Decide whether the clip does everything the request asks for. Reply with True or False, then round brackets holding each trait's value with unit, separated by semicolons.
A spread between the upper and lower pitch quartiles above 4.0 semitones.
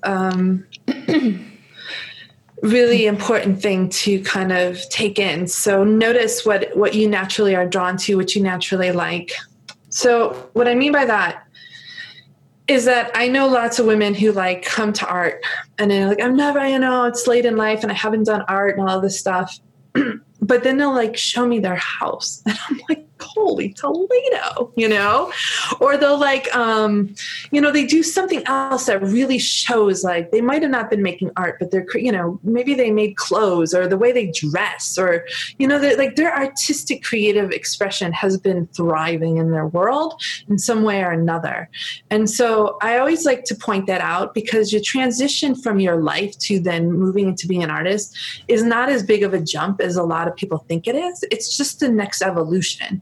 True (5.1 semitones)